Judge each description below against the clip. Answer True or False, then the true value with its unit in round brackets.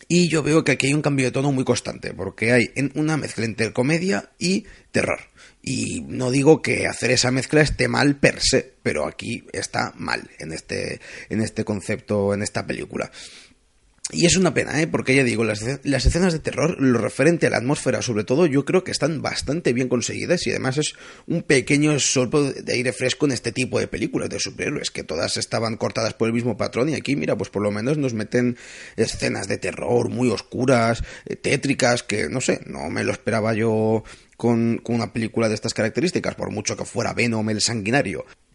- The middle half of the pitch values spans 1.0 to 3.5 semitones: False (4.0 semitones)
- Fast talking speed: True (205 wpm)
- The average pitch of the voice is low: True (125 Hz)